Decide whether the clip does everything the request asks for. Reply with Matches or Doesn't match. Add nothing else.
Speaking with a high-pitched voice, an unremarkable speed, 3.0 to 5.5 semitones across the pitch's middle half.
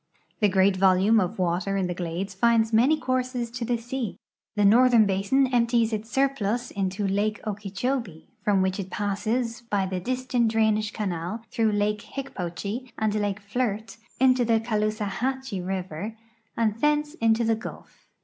Matches